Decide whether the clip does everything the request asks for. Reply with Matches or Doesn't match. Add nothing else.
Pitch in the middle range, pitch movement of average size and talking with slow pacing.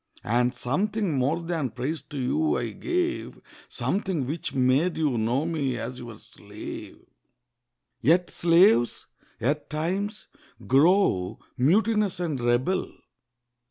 Doesn't match